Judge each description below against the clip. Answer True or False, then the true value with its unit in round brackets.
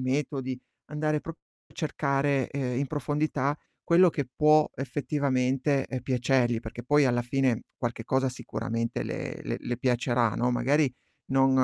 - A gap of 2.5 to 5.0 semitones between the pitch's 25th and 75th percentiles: True (2.8 semitones)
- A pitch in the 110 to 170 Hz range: True (135 Hz)